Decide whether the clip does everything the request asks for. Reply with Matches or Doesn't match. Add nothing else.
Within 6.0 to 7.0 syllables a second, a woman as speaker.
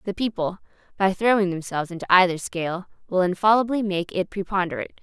Matches